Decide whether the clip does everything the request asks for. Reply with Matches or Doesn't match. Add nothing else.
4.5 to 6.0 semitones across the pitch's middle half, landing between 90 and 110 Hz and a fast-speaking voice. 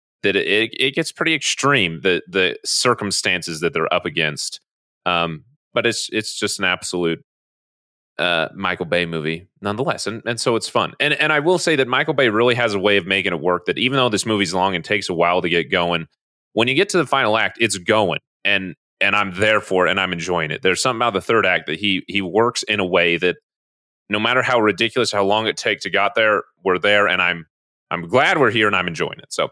Matches